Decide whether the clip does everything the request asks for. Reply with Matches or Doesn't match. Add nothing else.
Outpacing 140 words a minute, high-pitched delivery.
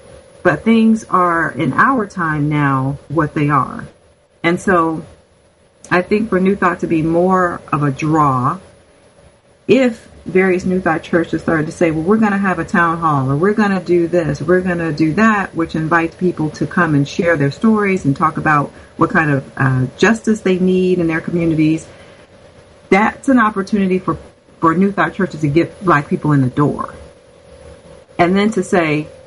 Doesn't match